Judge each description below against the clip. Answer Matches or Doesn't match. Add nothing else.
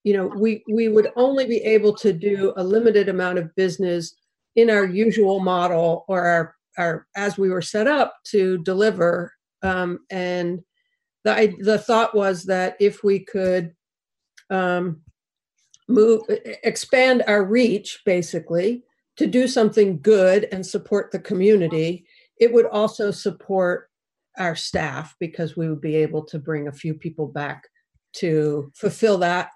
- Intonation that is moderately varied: Matches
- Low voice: Doesn't match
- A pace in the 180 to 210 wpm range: Doesn't match